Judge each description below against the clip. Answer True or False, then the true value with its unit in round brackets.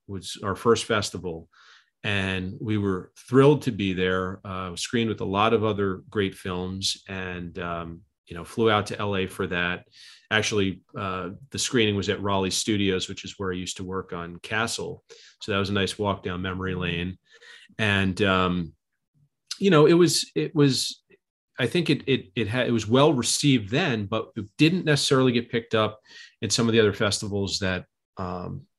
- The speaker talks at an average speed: True (190 wpm)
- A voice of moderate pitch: False (100 Hz)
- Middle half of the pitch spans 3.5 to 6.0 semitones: True (3.8 semitones)